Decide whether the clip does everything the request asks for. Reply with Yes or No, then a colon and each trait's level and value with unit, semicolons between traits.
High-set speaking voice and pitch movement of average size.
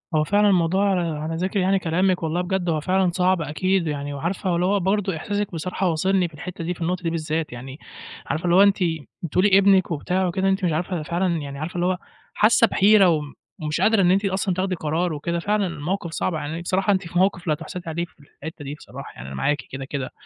No: medium, 175 Hz; average, 3.2 semitones